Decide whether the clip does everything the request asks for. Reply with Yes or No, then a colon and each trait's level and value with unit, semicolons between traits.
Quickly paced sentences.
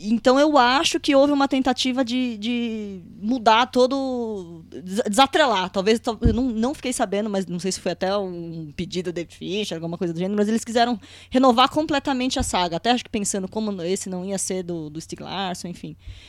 Yes: fast, 195 wpm